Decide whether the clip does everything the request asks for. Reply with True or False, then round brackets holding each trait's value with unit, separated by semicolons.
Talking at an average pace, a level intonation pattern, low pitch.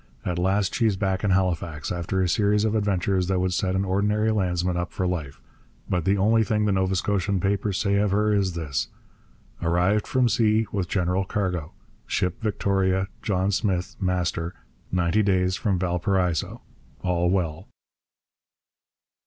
True (155 wpm; 2.3 semitones; 95 Hz)